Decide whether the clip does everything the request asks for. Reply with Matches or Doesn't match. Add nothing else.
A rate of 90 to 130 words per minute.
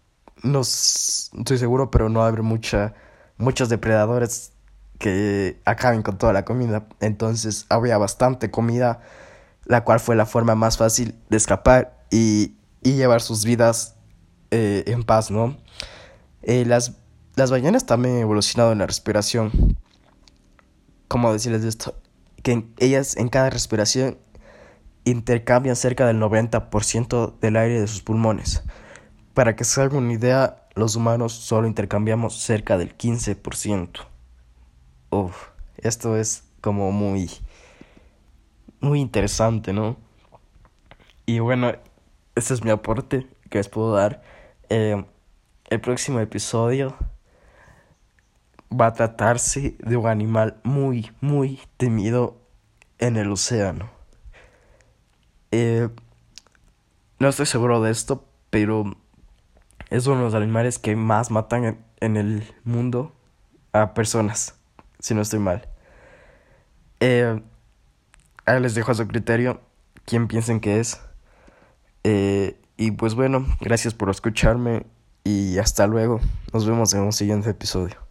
Matches